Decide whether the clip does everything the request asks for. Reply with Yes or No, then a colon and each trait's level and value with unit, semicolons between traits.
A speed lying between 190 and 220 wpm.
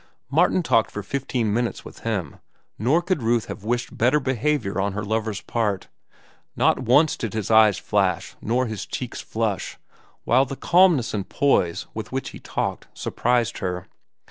No: average, 165 wpm